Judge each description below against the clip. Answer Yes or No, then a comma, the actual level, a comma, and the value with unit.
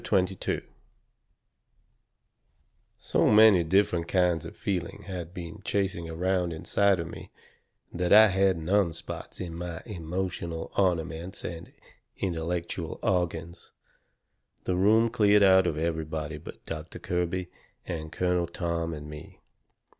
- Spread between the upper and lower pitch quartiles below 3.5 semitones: Yes, narrow, 2.4 semitones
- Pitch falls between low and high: No, very low, 90 Hz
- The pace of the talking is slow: Yes, slow, 125 wpm